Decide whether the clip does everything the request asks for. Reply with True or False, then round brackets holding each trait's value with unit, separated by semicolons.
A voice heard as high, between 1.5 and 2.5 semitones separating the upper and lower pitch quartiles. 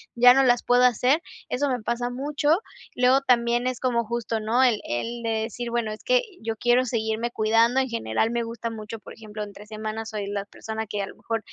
True (235 Hz; 2.2 semitones)